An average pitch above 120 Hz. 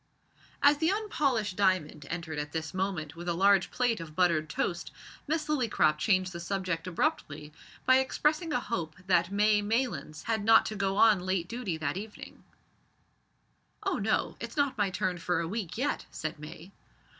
Yes: high, 190 Hz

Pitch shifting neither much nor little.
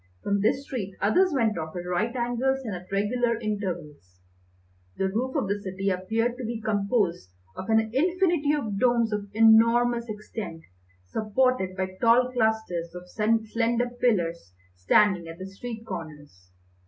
Yes: average, 4.3 semitones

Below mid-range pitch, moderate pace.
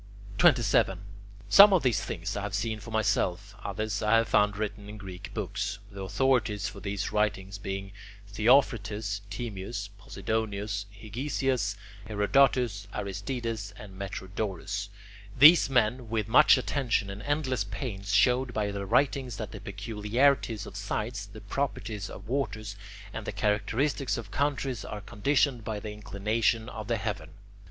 Yes: low, 105 Hz; average, 145 wpm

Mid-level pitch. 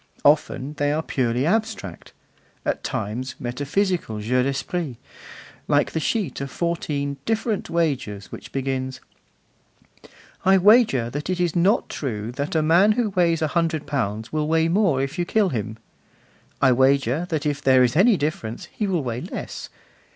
Yes: medium, 145 Hz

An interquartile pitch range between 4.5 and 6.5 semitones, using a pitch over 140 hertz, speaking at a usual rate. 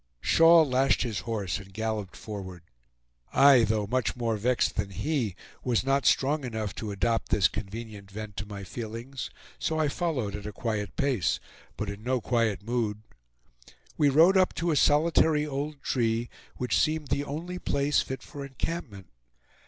No: average, 5.1 semitones; low, 120 Hz; average, 165 wpm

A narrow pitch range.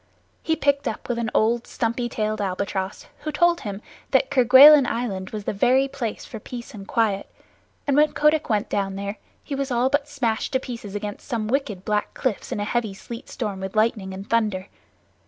No: average, 4.4 semitones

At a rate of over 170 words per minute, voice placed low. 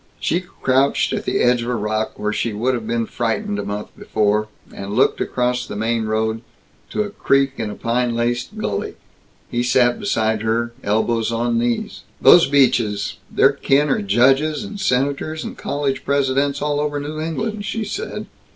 Yes: average, 180 wpm; low, 125 Hz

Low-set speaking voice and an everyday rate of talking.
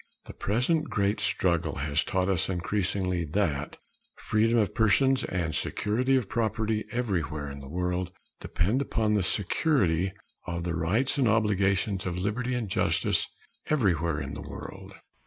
Yes: very low, 95 Hz; average, 145 wpm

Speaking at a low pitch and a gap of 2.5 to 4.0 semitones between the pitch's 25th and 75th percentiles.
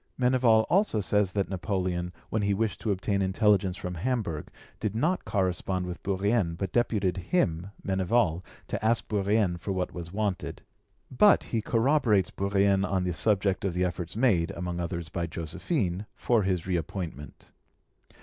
Yes: very low, 95 Hz; average, 3.3 semitones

